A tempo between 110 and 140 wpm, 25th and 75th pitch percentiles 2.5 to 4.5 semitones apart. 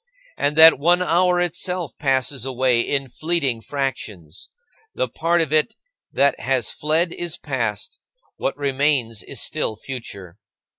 No: slow, 135 wpm; average, 4.9 semitones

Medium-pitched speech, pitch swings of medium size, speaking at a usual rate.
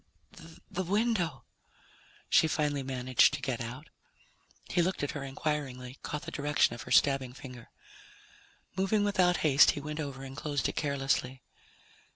Yes: medium, 145 Hz; average, 3.2 semitones; average, 150 wpm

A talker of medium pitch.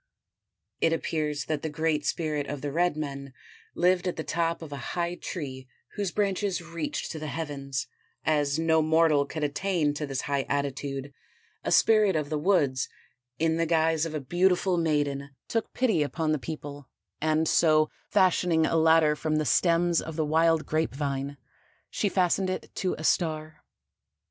Yes: medium, 155 Hz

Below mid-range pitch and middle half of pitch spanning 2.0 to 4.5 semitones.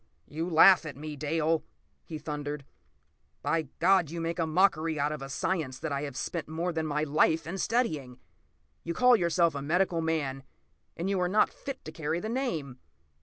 No: medium, 160 Hz; average, 2.9 semitones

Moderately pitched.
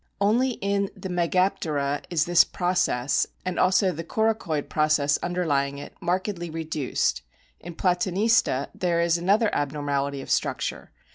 Yes: medium, 175 Hz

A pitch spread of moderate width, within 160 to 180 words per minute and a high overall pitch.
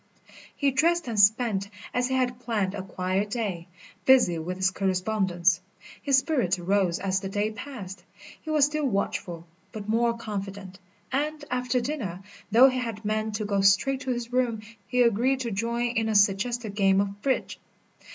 Yes: average, 4.4 semitones; average, 170 wpm; high, 215 Hz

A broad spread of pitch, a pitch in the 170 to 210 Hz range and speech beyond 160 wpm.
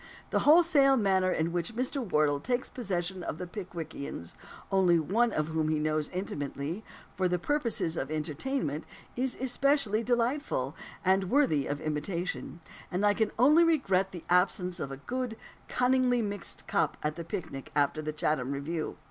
No: wide, 7.7 semitones; medium, 185 Hz; average, 155 wpm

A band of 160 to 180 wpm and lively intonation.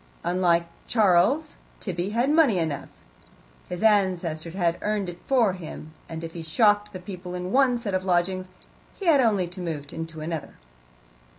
No: average, 165 wpm; average, 3.8 semitones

